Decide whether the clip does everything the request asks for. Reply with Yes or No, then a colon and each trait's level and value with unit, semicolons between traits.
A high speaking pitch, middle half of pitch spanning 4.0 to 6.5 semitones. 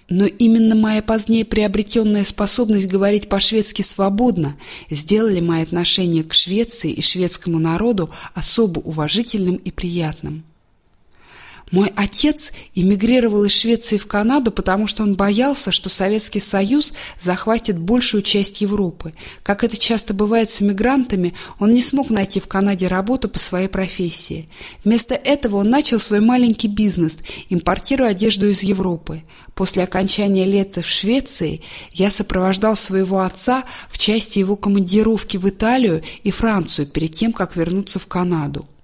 No: high, 200 Hz; average, 3.3 semitones